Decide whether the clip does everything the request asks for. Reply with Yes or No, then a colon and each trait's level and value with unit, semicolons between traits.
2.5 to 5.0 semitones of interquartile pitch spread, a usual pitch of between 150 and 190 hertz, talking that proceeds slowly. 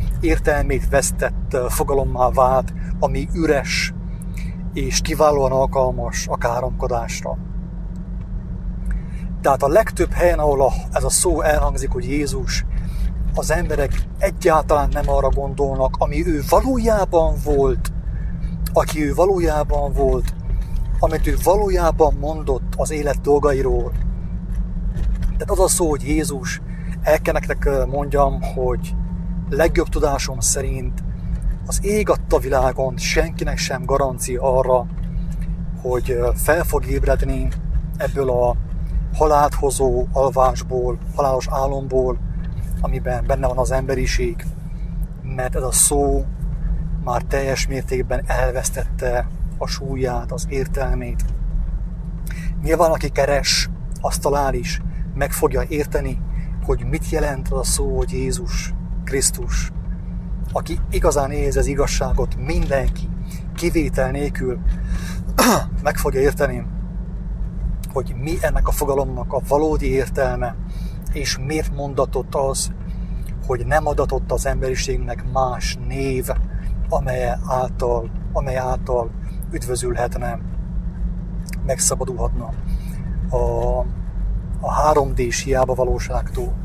No: average, 3.3 semitones; low, 135 Hz; slow, 105 wpm